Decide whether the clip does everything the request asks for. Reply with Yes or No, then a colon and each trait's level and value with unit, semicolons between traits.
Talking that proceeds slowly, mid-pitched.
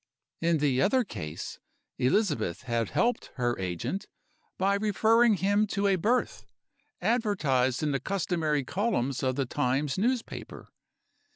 Yes: slow, 125 wpm; medium, 165 Hz